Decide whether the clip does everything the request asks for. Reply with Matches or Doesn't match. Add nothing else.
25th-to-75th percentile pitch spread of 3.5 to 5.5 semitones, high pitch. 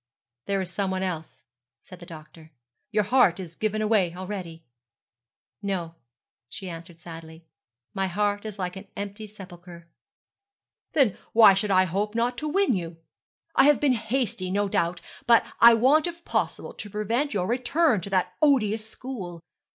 Matches